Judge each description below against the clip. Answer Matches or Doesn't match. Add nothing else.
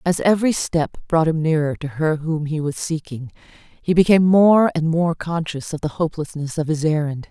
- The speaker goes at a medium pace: Matches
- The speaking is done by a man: Doesn't match